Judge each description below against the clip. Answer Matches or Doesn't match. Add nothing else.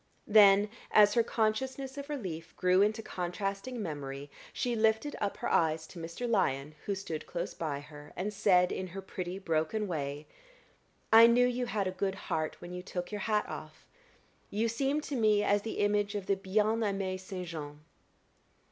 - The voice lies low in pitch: Doesn't match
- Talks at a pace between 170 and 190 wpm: Matches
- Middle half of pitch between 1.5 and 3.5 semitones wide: Doesn't match